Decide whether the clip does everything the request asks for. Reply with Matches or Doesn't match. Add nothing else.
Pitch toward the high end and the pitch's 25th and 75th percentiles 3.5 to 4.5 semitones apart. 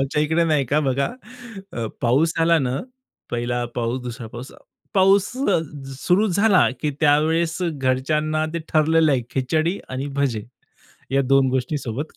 Doesn't match